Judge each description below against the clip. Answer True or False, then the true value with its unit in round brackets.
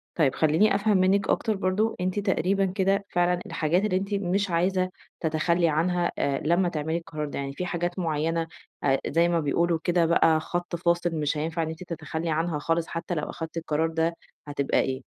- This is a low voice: False (170 Hz)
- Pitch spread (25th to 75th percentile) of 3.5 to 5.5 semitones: False (2.5 semitones)